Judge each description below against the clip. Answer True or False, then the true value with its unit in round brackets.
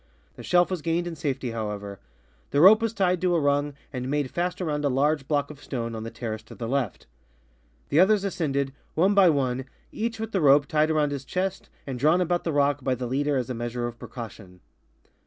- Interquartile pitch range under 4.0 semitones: False (5.5 semitones)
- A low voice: False (145 Hz)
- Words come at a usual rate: False (225 wpm)